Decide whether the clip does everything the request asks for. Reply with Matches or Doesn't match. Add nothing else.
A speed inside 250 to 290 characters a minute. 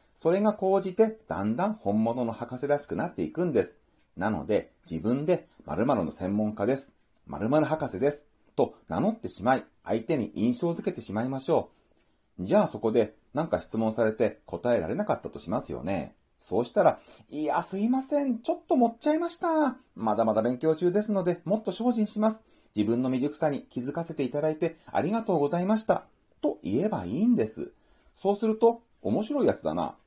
Doesn't match